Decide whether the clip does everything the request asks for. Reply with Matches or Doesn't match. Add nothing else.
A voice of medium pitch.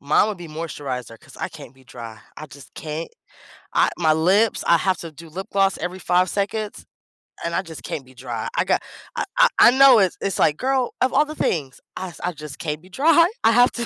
Matches